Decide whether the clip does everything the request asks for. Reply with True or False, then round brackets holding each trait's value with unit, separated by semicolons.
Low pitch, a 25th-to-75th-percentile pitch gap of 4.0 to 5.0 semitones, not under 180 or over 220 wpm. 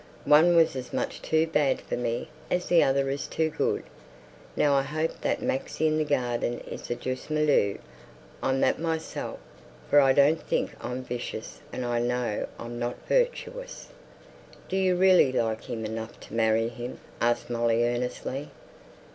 False (130 Hz; 4.7 semitones; 165 wpm)